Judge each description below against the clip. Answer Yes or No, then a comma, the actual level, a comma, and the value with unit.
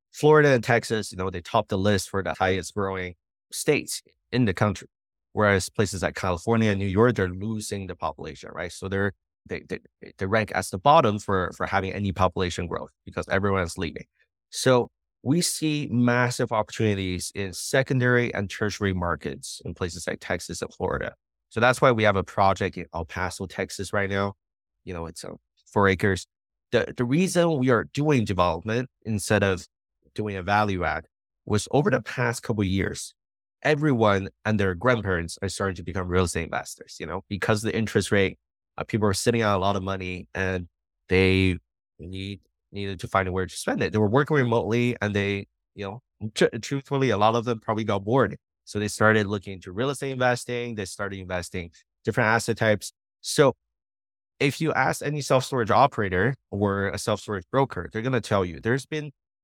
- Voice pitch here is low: Yes, low, 100 Hz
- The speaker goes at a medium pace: Yes, average, 190 wpm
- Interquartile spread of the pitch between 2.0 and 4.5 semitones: Yes, average, 3.9 semitones